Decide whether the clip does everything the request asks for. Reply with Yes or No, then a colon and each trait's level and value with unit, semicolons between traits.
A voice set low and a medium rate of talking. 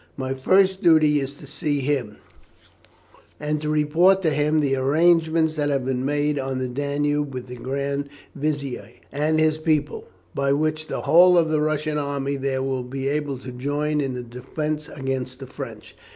No: medium, 145 Hz; average, 180 wpm